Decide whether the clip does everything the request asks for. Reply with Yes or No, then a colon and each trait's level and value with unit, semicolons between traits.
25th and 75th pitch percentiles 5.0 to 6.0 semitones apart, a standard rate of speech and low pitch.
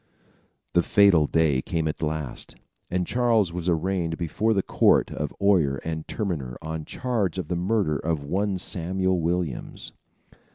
No: average, 3.5 semitones; average, 150 wpm; very low, 85 Hz